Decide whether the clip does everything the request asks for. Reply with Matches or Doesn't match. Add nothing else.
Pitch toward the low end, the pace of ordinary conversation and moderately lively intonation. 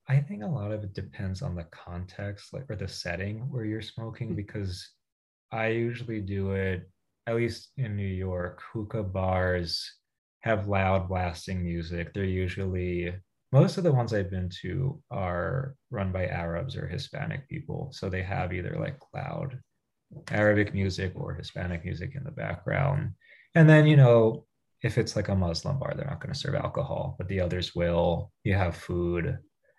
Matches